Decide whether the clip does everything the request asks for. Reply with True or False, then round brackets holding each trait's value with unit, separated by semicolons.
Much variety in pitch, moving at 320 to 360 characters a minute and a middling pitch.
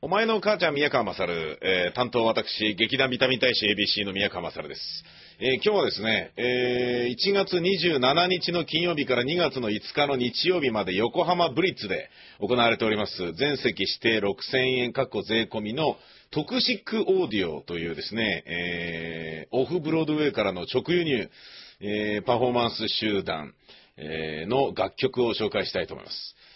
False (7.5 semitones; 325 characters per minute; 125 Hz)